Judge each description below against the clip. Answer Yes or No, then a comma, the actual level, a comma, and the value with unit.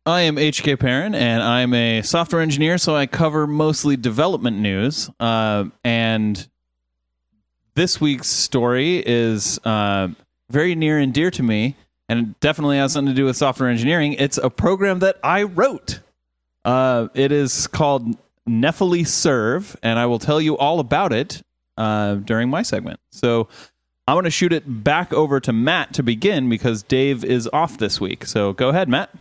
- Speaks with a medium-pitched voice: No, low, 130 Hz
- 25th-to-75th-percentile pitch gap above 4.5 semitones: Yes, average, 5.0 semitones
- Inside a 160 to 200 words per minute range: Yes, average, 170 wpm